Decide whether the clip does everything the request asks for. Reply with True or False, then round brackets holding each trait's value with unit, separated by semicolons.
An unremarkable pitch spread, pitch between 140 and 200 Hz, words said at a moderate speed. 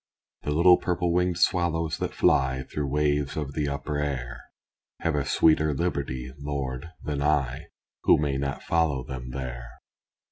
False (3.2 semitones; 75 Hz; 150 wpm)